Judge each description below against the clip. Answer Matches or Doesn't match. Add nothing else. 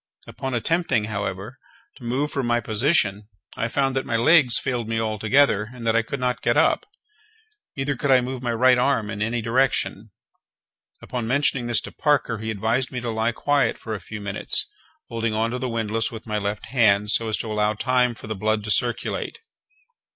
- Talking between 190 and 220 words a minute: Matches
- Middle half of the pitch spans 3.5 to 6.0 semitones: Doesn't match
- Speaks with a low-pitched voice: Matches